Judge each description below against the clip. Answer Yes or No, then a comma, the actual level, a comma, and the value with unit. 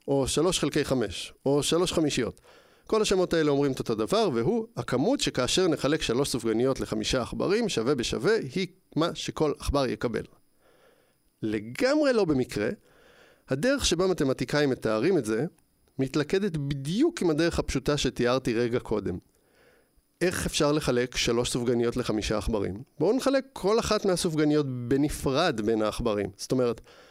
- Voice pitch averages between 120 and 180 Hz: Yes, medium, 140 Hz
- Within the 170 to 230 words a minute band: No, average, 140 wpm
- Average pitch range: No, wide, 6.0 semitones